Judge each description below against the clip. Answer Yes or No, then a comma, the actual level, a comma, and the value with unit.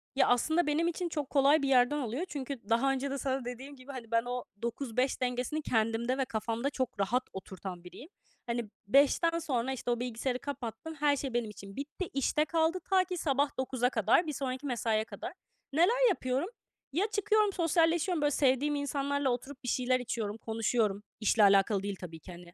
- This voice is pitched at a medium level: No, very high, 260 Hz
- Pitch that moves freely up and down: No, average, 4.2 semitones